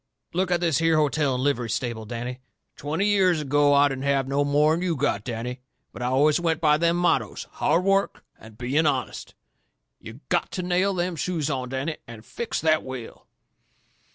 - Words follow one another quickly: No, average, 180 wpm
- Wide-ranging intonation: No, average, 4.6 semitones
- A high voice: No, medium, 145 Hz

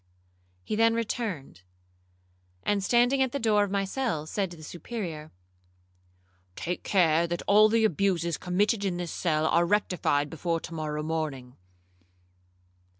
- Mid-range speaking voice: Yes, medium, 180 Hz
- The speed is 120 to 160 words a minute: Yes, average, 145 wpm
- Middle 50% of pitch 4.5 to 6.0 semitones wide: Yes, average, 4.9 semitones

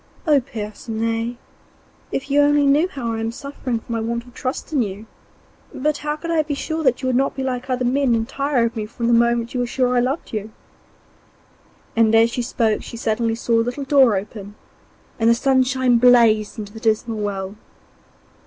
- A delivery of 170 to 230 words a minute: Yes, average, 200 wpm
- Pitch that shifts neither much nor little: Yes, average, 3.0 semitones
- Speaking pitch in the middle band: No, high, 240 Hz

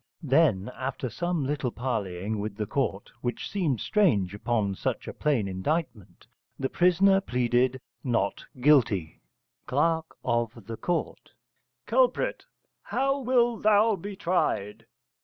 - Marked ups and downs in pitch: Yes, wide, 8.3 semitones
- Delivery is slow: Yes, slow, 120 wpm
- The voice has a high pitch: No, low, 130 Hz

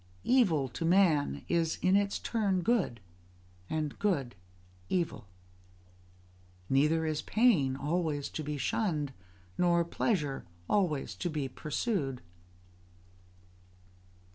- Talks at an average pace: No, slow, 100 wpm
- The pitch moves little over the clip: No, average, 4.6 semitones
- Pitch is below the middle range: No, medium, 160 Hz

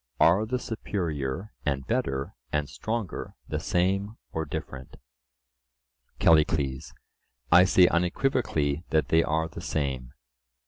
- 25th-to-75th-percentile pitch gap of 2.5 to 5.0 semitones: No, wide, 5.5 semitones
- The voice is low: Yes, very low, 80 Hz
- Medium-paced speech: No, slow, 110 wpm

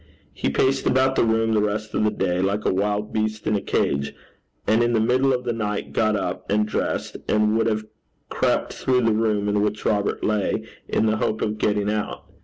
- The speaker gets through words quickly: Yes, fast, 215 wpm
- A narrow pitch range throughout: Yes, narrow, 1.5 semitones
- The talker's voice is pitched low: Yes, low, 105 Hz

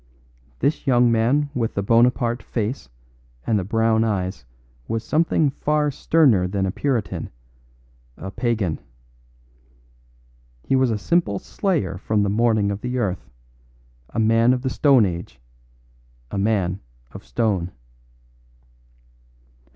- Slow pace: Yes, slow, 125 wpm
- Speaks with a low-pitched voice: Yes, low, 115 Hz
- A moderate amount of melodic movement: Yes, average, 4.3 semitones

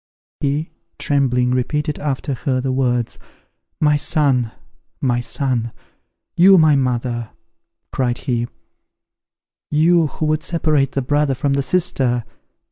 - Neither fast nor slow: No, slow, 120 wpm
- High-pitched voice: No, low, 135 Hz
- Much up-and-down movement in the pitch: No, average, 3.3 semitones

